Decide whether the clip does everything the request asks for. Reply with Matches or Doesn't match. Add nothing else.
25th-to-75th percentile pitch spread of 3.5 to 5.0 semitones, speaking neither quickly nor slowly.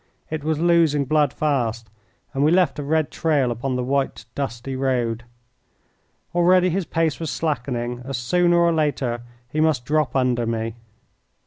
Matches